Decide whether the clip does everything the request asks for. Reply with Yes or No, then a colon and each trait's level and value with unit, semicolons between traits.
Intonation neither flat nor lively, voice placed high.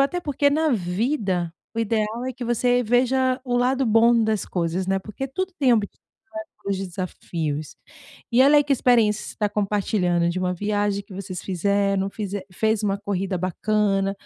Yes: average, 4.4 semitones; high, 210 Hz